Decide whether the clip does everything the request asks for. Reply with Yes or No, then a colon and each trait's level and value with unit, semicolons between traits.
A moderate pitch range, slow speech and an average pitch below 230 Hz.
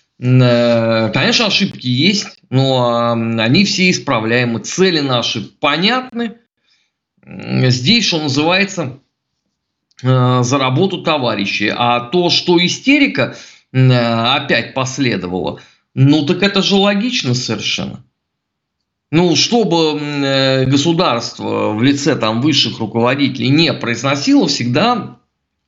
No: wide, 6.5 semitones; slow, 90 wpm; low, 135 Hz